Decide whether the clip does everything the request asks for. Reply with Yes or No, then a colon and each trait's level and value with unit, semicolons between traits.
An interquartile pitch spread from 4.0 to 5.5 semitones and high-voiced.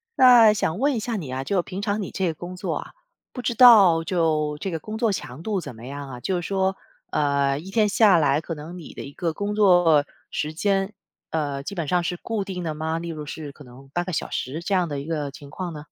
No: average, 4.8 semitones; medium, 170 Hz